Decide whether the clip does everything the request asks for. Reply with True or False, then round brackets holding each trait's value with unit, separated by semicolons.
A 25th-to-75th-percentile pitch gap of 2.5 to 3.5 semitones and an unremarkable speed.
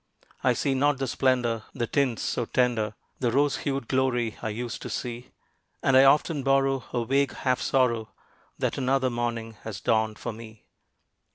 True (2.8 semitones; 170 wpm)